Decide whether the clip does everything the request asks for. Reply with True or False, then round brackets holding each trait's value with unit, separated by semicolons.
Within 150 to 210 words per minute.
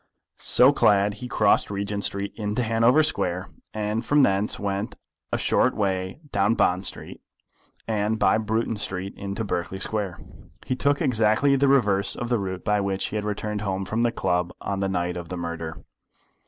True (180 wpm)